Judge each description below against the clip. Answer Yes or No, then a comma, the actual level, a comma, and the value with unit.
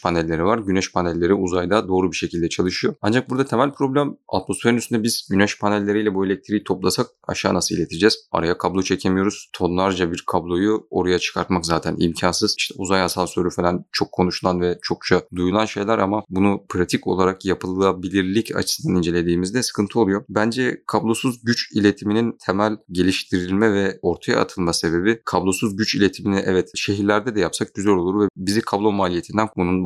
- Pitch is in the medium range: No, very low, 95 Hz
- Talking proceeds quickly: Yes, fast, 155 wpm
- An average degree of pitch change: Yes, average, 3.0 semitones